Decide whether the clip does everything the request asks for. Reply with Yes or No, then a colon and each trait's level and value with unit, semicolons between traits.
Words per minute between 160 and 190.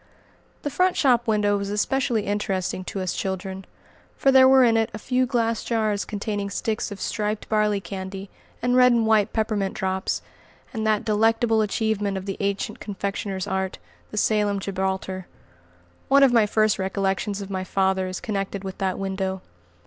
Yes: average, 170 wpm